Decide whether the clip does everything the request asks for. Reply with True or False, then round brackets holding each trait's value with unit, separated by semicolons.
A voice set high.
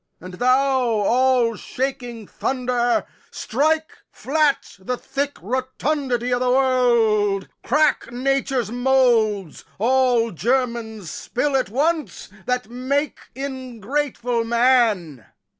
True (250 Hz)